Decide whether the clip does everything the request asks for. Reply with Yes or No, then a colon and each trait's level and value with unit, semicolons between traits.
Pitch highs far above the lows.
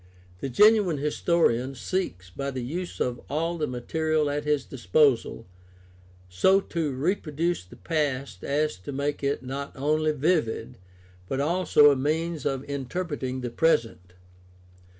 No: average, 3.8 semitones